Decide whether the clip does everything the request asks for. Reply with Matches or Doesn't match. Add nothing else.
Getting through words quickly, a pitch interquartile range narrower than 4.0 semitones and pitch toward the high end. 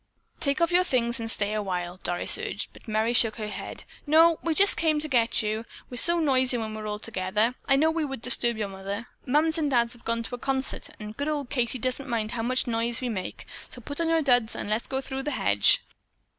Doesn't match